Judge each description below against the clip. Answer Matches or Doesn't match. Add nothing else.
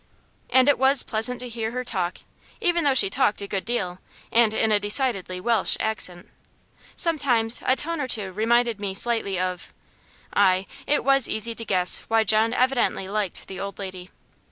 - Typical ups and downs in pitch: Matches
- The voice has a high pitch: Matches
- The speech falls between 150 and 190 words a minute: Matches